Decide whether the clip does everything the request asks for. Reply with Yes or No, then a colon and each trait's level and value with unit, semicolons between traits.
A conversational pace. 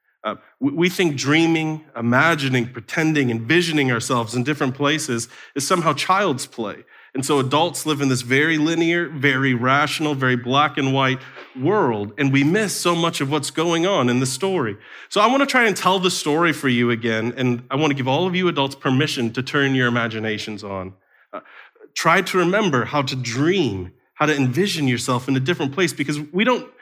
Yes: average, 195 wpm